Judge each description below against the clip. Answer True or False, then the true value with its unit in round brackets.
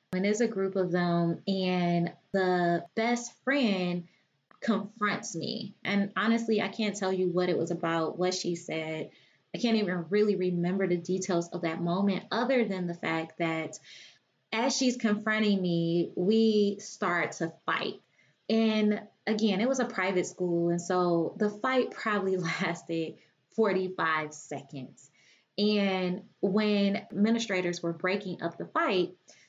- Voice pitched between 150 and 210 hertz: True (185 Hz)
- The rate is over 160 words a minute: False (145 wpm)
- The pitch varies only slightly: False (3.5 semitones)